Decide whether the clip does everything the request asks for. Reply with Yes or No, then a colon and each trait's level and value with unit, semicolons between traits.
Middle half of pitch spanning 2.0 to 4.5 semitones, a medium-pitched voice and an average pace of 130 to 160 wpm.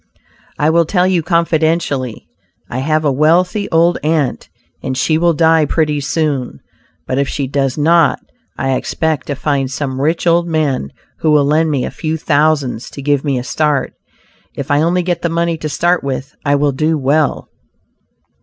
No: average, 2.8 semitones; medium, 155 Hz; average, 180 wpm